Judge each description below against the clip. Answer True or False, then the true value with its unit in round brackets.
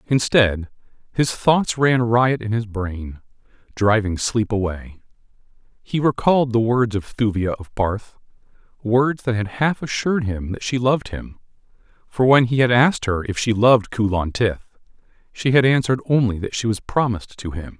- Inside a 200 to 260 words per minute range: False (170 wpm)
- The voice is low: True (115 Hz)